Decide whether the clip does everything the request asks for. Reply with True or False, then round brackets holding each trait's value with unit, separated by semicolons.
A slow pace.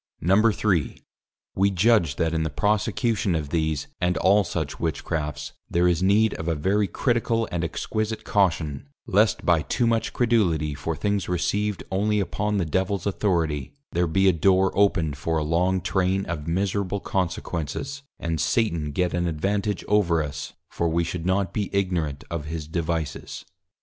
False (165 wpm)